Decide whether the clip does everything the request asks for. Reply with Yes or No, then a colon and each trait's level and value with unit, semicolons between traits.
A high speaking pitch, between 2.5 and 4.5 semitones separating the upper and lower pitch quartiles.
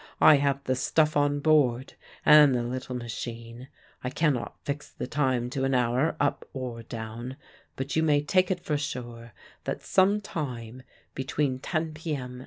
No: low, 135 Hz; average, 3.4 semitones